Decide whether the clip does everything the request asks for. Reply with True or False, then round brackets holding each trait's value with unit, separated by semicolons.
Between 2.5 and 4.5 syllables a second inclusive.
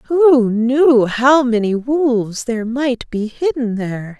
True (3.6 syllables/s)